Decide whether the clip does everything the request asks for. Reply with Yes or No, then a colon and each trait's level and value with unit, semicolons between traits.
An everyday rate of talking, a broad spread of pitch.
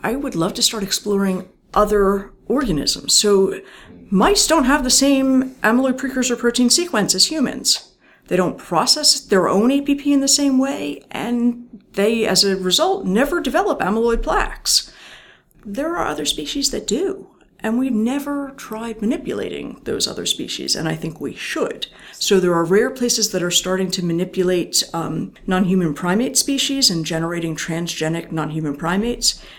Yes: average, 160 wpm; wide, 6.5 semitones